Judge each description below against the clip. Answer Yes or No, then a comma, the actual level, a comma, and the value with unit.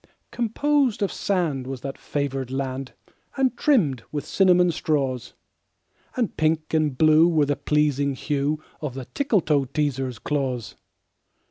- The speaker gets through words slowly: Yes, slow, 125 wpm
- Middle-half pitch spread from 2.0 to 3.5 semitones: No, average, 4.4 semitones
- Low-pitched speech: No, medium, 150 Hz